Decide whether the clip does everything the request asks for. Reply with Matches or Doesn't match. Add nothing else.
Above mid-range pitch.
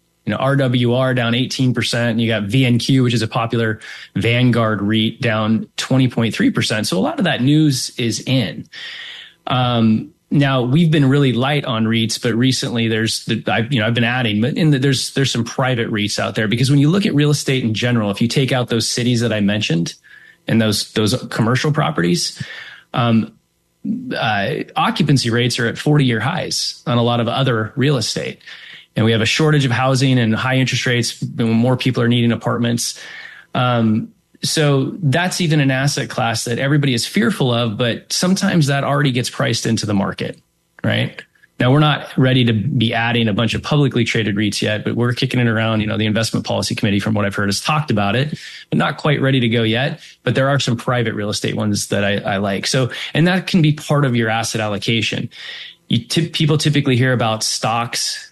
Doesn't match